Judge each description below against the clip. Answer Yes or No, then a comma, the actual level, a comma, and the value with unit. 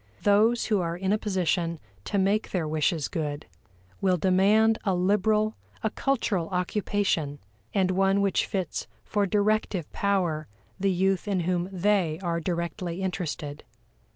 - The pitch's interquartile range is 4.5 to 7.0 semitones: No, average, 3.1 semitones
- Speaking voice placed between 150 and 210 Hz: Yes, high, 190 Hz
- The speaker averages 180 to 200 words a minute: No, average, 140 wpm